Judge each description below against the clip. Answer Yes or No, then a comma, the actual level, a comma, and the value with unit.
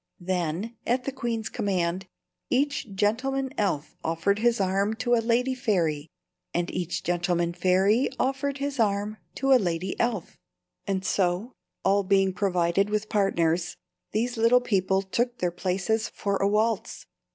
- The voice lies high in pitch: Yes, high, 200 Hz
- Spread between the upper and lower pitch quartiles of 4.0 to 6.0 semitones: Yes, average, 4.7 semitones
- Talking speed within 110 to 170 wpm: Yes, average, 145 wpm